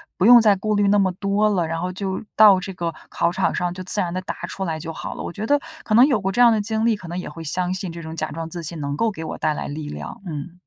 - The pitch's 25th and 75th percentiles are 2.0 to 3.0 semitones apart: No, average, 3.8 semitones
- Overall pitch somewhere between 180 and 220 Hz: Yes, medium, 185 Hz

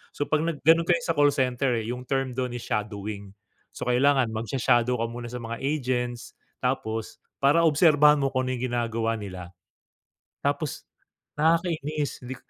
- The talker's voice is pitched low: Yes, low, 130 Hz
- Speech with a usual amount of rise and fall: Yes, average, 3.8 semitones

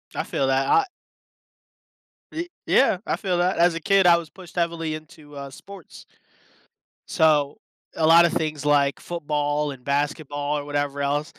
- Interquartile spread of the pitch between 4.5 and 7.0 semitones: No, average, 2.9 semitones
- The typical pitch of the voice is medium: Yes, medium, 150 Hz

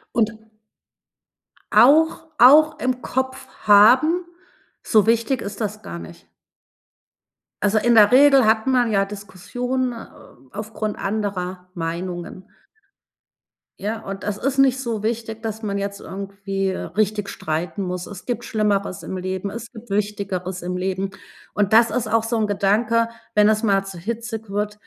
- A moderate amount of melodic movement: Yes, average, 3.1 semitones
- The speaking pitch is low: No, high, 210 Hz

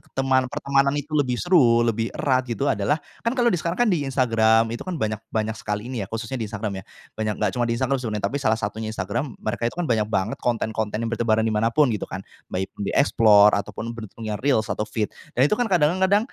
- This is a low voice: Yes, low, 115 Hz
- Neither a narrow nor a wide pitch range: Yes, average, 4.2 semitones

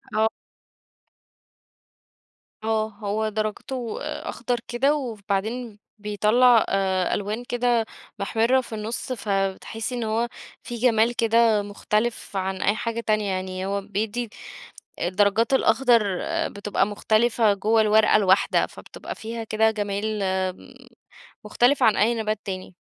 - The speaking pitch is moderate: No, high, 220 Hz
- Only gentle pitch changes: Yes, narrow, 2.3 semitones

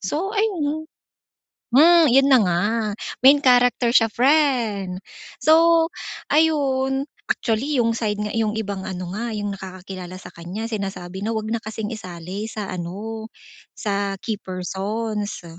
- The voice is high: Yes, high, 220 Hz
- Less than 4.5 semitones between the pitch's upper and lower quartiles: No, average, 5.2 semitones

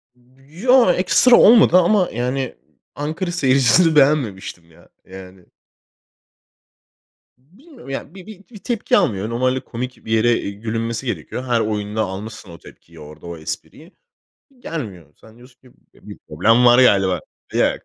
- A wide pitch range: Yes, wide, 7.4 semitones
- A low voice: Yes, low, 120 Hz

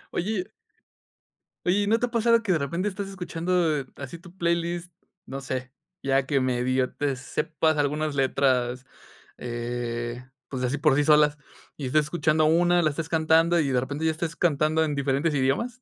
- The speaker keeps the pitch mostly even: No, average, 4.3 semitones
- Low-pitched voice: No, medium, 155 Hz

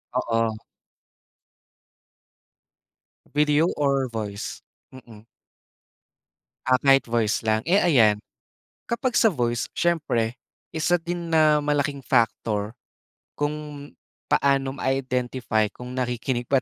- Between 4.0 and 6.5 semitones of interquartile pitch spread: Yes, average, 4.3 semitones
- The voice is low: Yes, low, 130 Hz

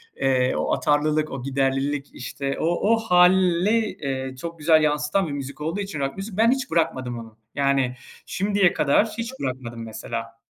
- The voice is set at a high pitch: No, medium, 145 Hz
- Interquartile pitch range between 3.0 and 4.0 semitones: No, average, 5.3 semitones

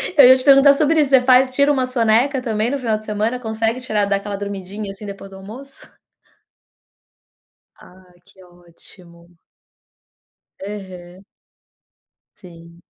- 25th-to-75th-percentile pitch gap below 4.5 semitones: No, average, 5.1 semitones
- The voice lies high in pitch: Yes, high, 215 Hz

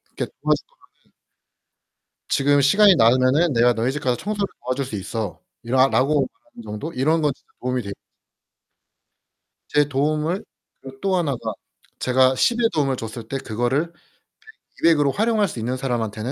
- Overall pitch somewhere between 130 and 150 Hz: Yes, low, 135 Hz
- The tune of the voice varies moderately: Yes, average, 4.1 semitones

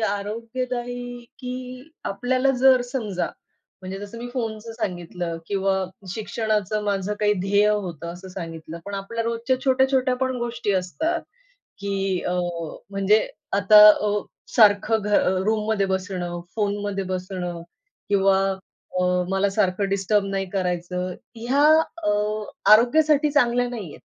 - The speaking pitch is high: Yes, high, 205 Hz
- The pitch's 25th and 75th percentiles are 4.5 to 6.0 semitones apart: No, average, 3.9 semitones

